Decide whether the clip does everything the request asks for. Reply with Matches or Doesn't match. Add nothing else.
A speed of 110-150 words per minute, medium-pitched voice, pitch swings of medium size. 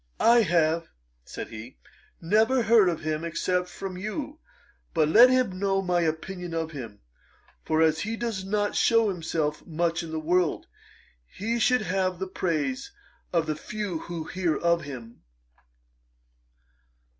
Matches